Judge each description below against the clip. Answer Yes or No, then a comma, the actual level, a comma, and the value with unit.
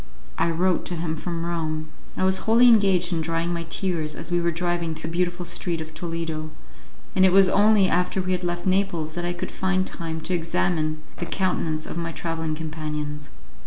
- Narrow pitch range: Yes, narrow, 2.3 semitones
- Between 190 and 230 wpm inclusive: Yes, average, 200 wpm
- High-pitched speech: No, medium, 170 Hz